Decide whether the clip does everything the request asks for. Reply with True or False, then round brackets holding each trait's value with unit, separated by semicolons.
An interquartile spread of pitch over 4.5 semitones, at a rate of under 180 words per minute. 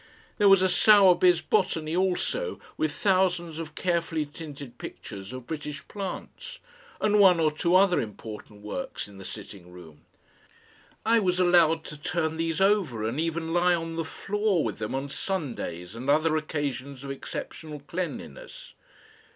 True (5.0 semitones; 150 wpm)